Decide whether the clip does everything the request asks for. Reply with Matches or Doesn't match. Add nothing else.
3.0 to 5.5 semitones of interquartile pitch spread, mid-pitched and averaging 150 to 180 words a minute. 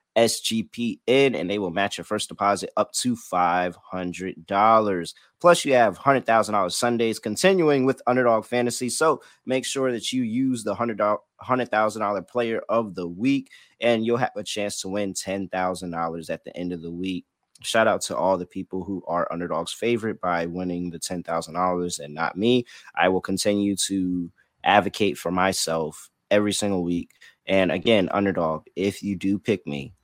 Doesn't match